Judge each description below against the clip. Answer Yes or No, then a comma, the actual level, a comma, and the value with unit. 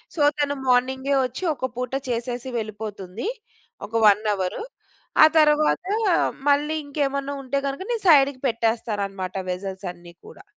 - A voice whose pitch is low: No, very high, 250 Hz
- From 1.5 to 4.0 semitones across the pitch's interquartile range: No, wide, 5.5 semitones